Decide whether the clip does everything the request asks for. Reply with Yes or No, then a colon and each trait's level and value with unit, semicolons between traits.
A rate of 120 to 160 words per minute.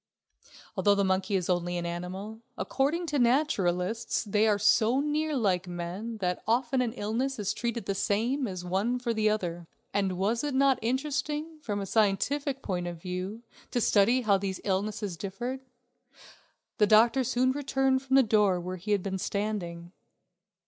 No: average, 170 wpm